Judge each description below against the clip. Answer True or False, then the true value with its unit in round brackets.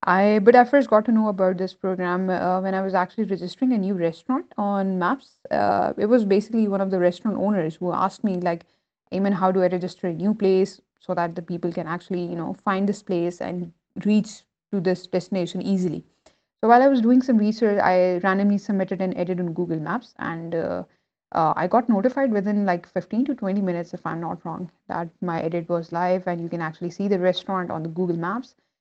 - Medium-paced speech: False (220 wpm)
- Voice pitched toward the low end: False (190 Hz)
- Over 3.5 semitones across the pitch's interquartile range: False (2.8 semitones)